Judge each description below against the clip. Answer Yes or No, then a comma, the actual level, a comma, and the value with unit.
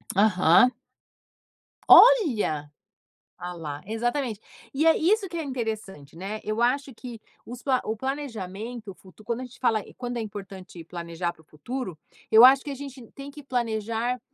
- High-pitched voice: Yes, high, 230 Hz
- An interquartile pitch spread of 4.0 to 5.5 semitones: Yes, average, 5.2 semitones